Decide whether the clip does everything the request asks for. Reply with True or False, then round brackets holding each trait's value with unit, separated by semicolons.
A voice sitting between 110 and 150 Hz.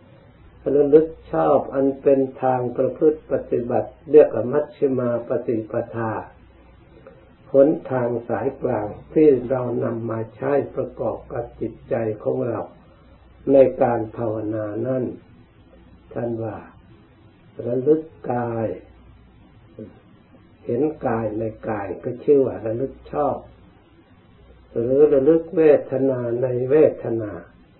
True (120 Hz)